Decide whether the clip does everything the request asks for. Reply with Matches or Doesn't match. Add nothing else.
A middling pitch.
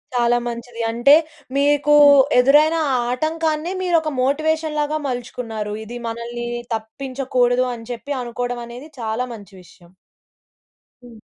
Doesn't match